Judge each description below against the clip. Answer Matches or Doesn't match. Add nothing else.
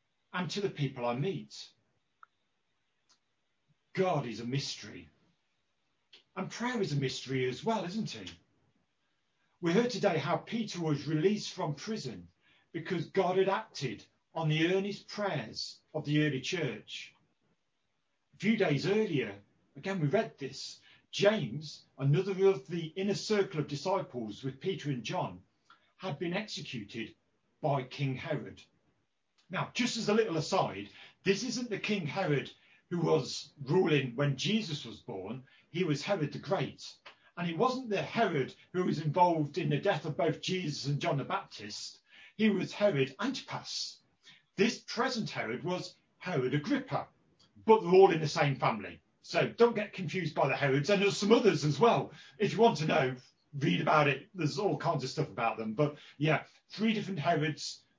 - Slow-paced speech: Doesn't match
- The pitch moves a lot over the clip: Matches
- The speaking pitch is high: Doesn't match